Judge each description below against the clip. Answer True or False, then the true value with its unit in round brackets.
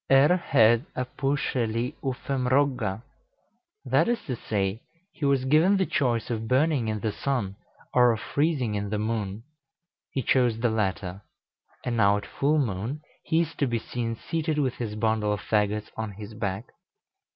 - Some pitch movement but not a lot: True (4.5 semitones)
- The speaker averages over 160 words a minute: True (170 wpm)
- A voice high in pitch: False (120 Hz)